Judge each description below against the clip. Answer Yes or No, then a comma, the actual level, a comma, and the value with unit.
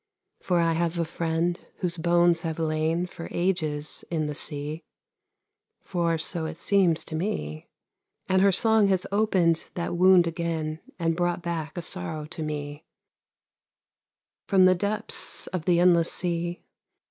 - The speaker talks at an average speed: Yes, average, 145 wpm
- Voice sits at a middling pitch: Yes, medium, 170 Hz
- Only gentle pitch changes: Yes, narrow, 2.0 semitones